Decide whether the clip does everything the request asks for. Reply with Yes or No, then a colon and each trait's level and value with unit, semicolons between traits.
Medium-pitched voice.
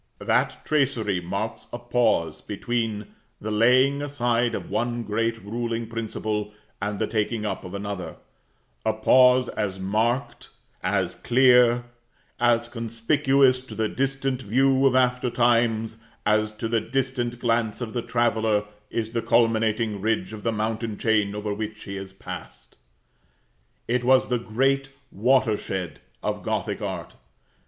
No: low, 115 Hz